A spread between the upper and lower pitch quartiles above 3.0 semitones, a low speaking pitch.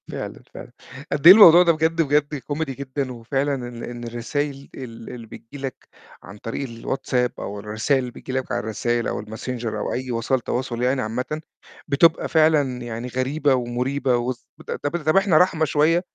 Yes: average, 3.6 semitones; low, 130 Hz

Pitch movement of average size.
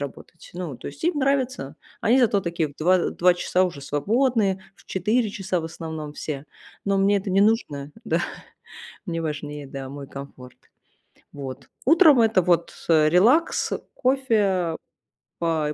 No: wide, 6.6 semitones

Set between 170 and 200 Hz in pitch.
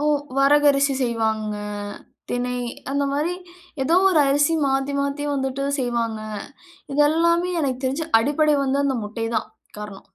No: very high, 275 Hz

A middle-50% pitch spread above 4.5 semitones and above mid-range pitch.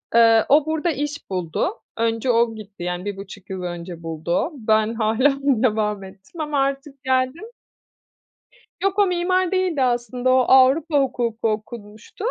Yes: average, 5.2 semitones; high, 240 Hz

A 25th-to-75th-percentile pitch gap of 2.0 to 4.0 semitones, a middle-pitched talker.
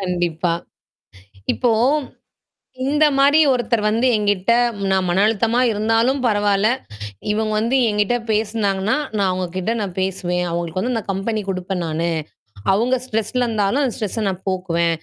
No: average, 3.5 semitones; high, 205 Hz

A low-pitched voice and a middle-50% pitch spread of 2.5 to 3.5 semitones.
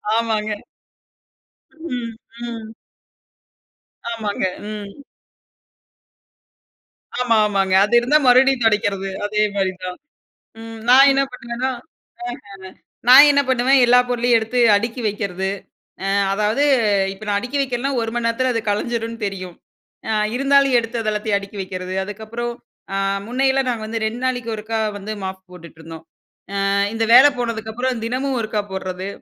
No: high, 225 Hz; average, 3.2 semitones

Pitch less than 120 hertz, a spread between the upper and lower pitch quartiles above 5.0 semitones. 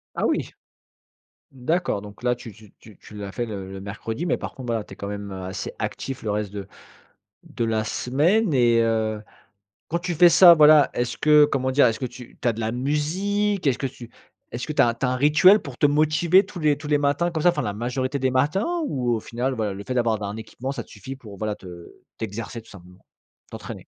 No: low, 125 Hz; wide, 5.4 semitones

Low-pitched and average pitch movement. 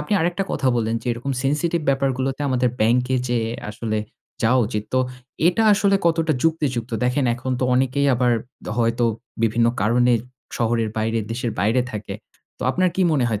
Yes: low, 125 Hz; average, 3.4 semitones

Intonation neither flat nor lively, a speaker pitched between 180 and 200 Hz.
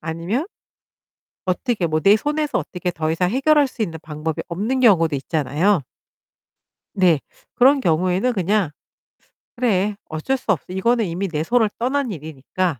No: wide, 6.8 semitones; high, 190 Hz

